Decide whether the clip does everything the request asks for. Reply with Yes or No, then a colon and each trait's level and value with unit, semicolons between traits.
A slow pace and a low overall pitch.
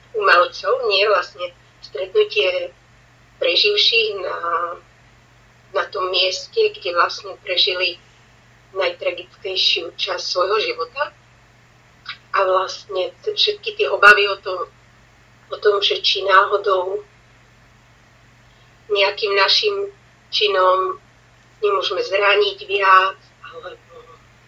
No: slow, 85 wpm; high, 195 Hz